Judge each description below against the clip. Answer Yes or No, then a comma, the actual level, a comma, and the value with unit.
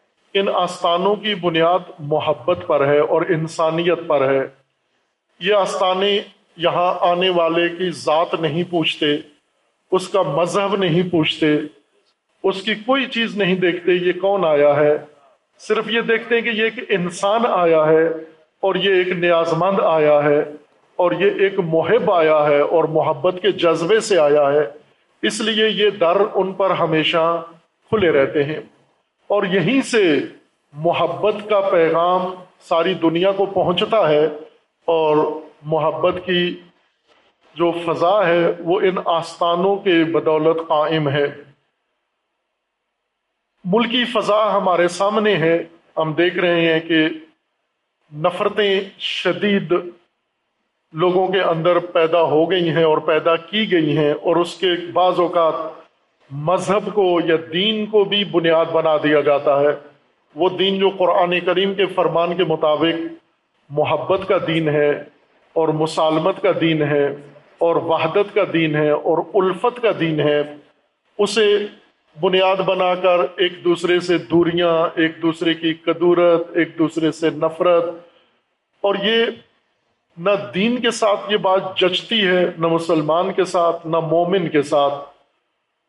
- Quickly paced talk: No, average, 140 wpm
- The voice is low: No, medium, 170 Hz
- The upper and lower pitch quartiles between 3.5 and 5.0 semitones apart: No, average, 3.0 semitones